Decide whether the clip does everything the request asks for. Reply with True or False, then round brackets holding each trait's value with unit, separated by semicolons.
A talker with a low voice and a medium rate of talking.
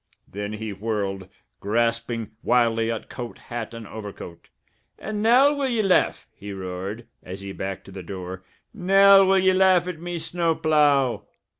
True (115 Hz; 160 wpm)